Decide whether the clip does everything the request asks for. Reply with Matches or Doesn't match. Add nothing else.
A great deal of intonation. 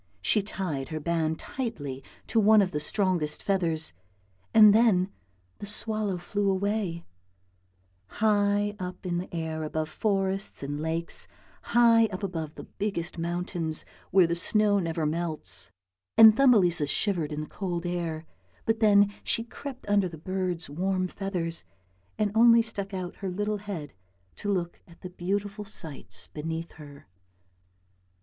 Doesn't match